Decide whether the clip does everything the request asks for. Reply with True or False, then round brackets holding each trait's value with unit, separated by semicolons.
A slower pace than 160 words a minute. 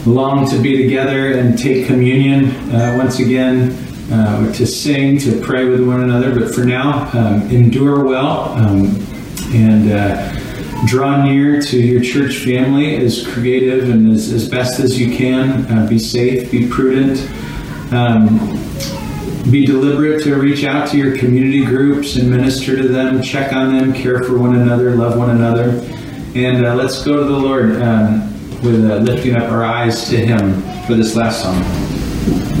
False (165 wpm)